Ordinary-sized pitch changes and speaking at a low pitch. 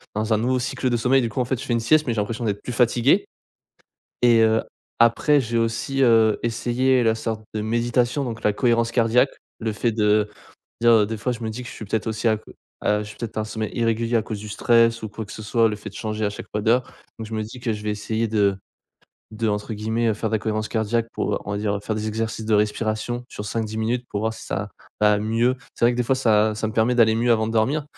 No: narrow, 1.7 semitones; low, 110 Hz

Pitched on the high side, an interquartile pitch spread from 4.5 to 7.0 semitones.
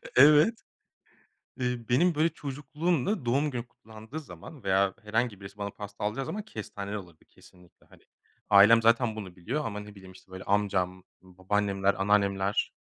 No: low, 105 Hz; average, 4.9 semitones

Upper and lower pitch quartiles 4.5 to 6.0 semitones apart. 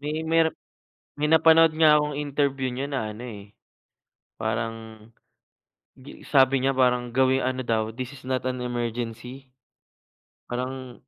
No: average, 2.9 semitones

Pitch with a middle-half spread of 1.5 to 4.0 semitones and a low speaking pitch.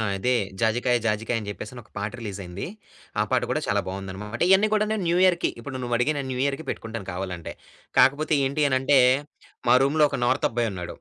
No: wide, 5.4 semitones; low, 120 Hz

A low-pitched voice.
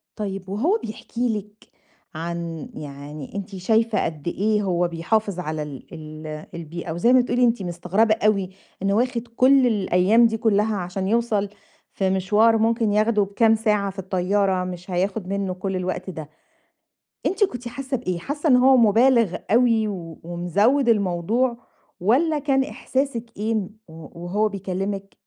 No: high, 200 Hz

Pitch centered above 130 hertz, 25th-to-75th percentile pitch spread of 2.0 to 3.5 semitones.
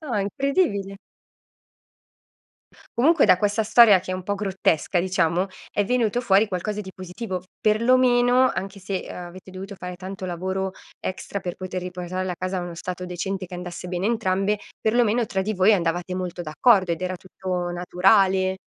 Yes: high, 190 Hz; narrow, 2.6 semitones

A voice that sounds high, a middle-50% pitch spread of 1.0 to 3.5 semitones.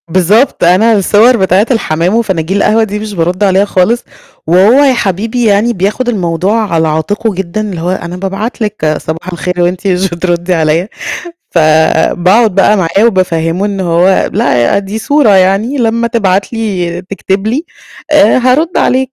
No: high, 195 Hz; average, 4.0 semitones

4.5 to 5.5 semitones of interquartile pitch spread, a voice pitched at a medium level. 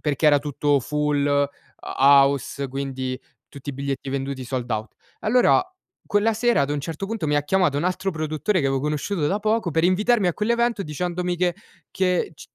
Yes: average, 5.2 semitones; medium, 150 Hz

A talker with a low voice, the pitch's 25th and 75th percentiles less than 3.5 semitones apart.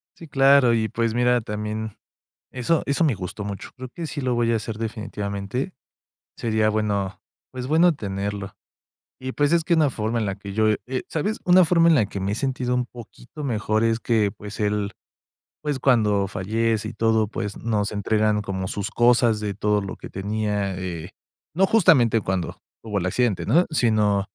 No: low, 110 Hz; average, 3.8 semitones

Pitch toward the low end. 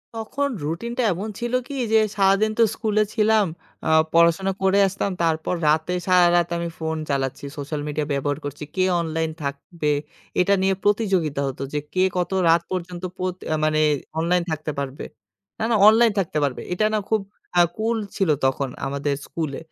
No: medium, 175 Hz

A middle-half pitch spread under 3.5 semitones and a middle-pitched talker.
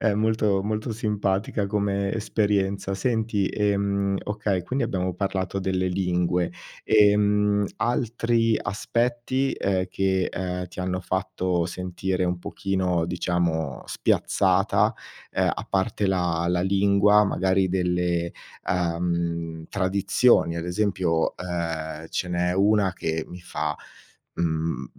No: narrow, 2.6 semitones; very low, 95 Hz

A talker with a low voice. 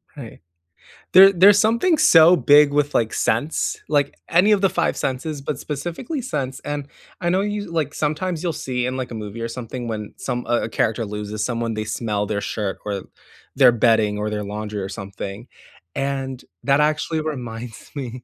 Yes: low, 130 Hz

